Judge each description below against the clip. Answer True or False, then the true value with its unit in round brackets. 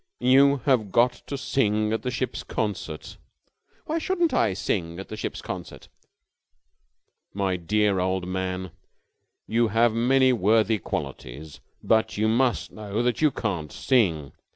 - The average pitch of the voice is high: False (110 Hz)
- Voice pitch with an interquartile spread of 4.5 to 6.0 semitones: True (4.8 semitones)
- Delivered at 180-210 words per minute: False (140 wpm)